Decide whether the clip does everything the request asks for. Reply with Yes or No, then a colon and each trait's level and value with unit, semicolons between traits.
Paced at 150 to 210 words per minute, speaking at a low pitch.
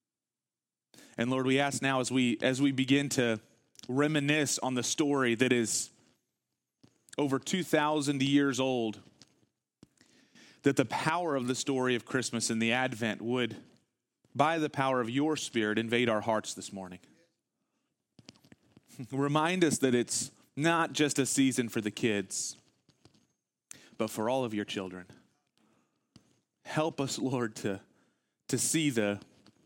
No: average, 140 wpm; low, 130 Hz